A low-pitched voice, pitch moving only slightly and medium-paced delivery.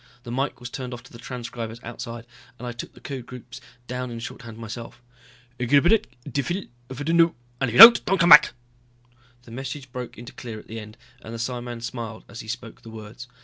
No: low, 120 Hz; narrow, 2.3 semitones; fast, 210 wpm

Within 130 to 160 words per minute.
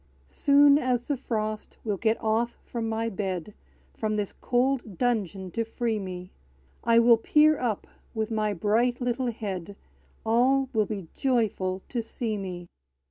Yes: average, 150 wpm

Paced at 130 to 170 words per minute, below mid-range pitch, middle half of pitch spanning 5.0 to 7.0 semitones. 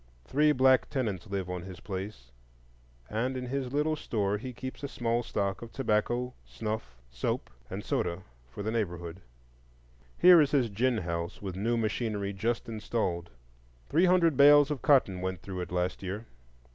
Yes: average, 165 wpm; low, 110 Hz; wide, 5.6 semitones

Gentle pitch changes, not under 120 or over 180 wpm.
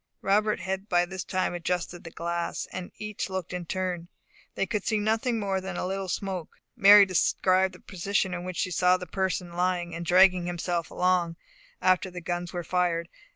No: narrow, 1.6 semitones; average, 190 wpm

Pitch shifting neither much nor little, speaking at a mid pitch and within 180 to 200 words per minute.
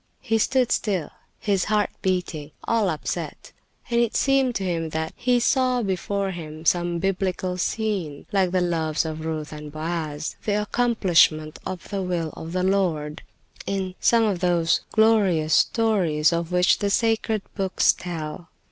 No: average, 4.5 semitones; medium, 180 Hz; average, 155 wpm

